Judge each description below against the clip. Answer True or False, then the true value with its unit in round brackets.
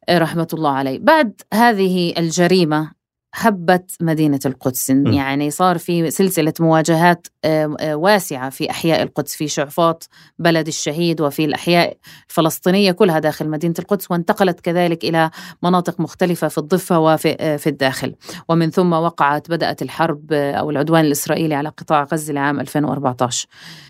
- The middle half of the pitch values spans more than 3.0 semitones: False (2.6 semitones)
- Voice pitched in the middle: True (160 Hz)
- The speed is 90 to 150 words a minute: True (130 wpm)